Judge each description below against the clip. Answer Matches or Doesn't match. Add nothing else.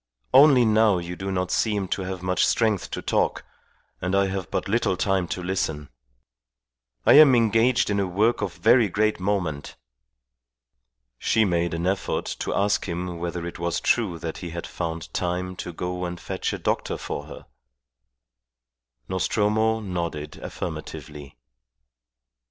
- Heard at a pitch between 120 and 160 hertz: Doesn't match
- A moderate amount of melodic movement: Matches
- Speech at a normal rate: Matches